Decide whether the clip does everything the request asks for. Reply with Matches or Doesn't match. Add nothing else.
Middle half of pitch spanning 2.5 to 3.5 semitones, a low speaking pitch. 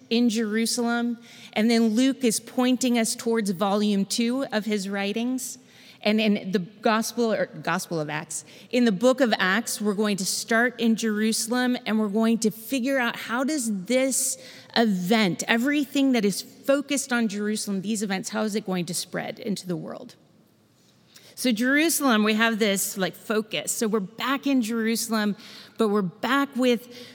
Doesn't match